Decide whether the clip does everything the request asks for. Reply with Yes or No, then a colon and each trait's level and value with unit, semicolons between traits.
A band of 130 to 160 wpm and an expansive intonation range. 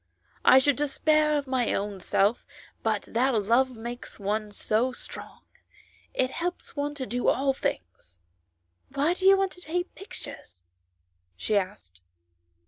Yes: average, 155 wpm; wide, 6.5 semitones